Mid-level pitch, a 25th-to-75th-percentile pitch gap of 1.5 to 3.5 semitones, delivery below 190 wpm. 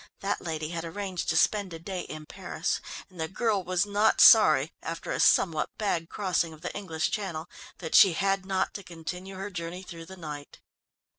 No: medium, 180 Hz; average, 3.1 semitones; average, 195 wpm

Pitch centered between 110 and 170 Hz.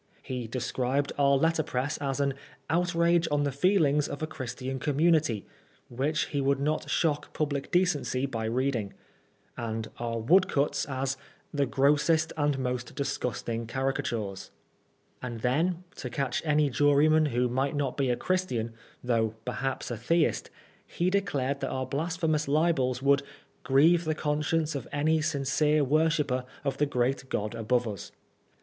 Yes: medium, 140 Hz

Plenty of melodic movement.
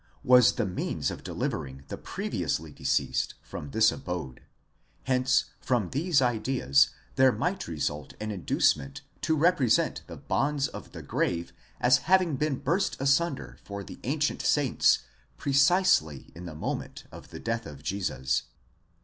Yes: wide, 8.7 semitones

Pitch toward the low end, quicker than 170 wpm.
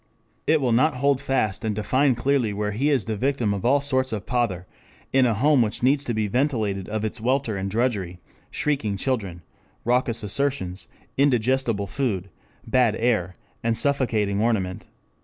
No: low, 115 Hz; average, 165 wpm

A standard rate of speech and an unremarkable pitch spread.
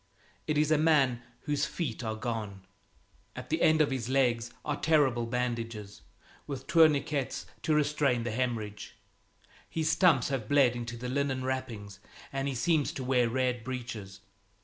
Yes: average, 155 wpm; average, 3.7 semitones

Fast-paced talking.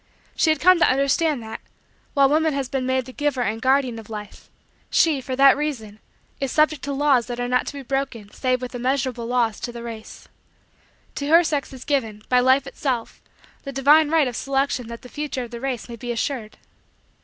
Yes: fast, 210 wpm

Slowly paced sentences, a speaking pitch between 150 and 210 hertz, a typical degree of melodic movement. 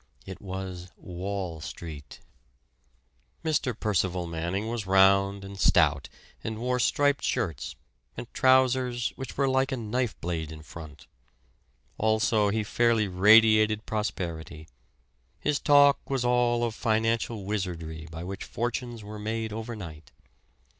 No: slow, 125 wpm; low, 105 Hz; average, 4.8 semitones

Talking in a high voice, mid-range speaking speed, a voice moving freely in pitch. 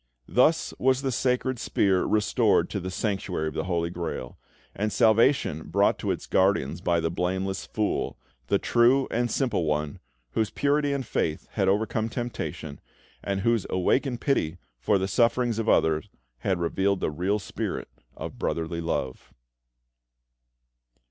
No: low, 100 Hz; average, 150 wpm; wide, 5.8 semitones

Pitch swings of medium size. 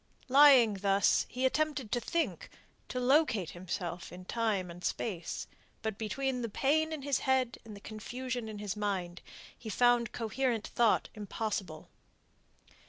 Yes: average, 4.5 semitones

